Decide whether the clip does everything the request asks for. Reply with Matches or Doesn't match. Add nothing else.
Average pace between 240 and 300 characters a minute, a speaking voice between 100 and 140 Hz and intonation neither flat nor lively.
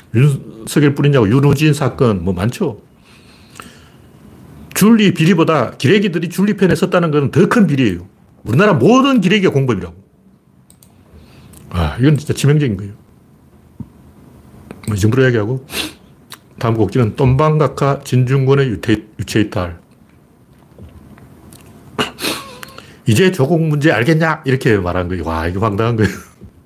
Doesn't match